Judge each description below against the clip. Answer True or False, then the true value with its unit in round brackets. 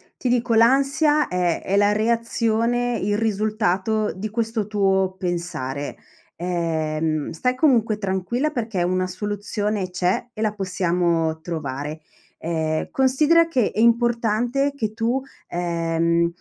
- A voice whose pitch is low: False (205 Hz)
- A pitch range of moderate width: True (5.0 semitones)